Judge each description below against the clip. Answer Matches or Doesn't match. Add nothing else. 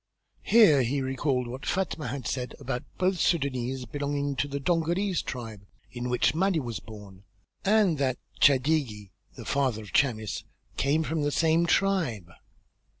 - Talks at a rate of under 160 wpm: Matches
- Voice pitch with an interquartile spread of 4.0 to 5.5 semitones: Matches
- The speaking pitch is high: Doesn't match